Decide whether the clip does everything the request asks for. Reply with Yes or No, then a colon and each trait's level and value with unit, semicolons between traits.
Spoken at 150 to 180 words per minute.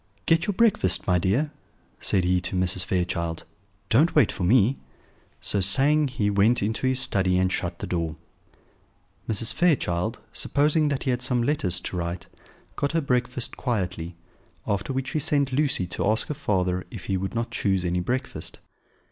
Yes: average, 175 wpm